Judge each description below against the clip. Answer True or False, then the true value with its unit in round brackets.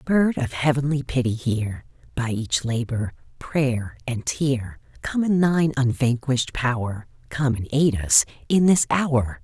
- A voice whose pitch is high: False (130 Hz)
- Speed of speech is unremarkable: True (145 wpm)